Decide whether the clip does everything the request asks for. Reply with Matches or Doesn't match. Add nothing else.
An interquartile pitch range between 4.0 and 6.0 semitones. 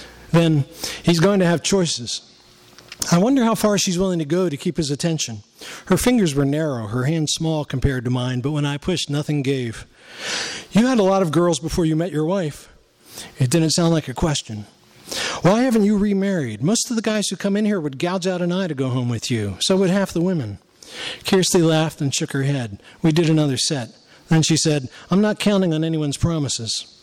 Matches